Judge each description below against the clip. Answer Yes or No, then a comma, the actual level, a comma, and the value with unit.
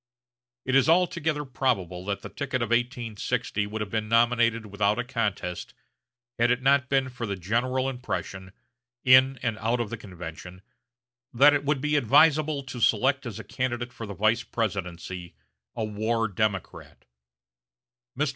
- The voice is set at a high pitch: No, low, 115 Hz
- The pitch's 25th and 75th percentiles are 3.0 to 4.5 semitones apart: Yes, average, 3.9 semitones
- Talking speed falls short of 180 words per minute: Yes, average, 155 wpm